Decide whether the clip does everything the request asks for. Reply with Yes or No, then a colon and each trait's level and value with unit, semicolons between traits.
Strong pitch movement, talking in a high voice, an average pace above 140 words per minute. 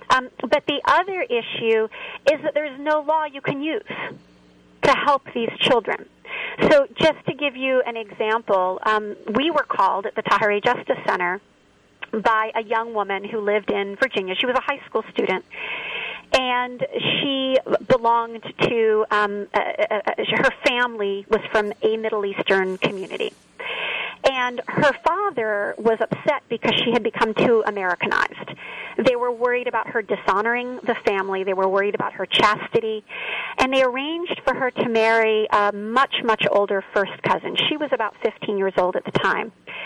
Yes: wide, 5.8 semitones; high, 235 Hz; average, 165 wpm